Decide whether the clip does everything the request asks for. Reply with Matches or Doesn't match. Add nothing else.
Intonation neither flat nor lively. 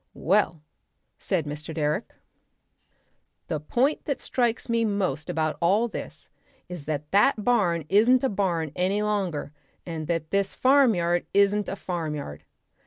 Matches